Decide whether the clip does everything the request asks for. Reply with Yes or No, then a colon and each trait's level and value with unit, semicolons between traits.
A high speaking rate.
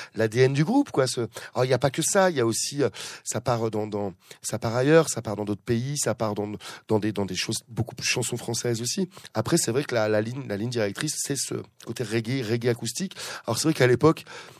Yes: fast, 250 wpm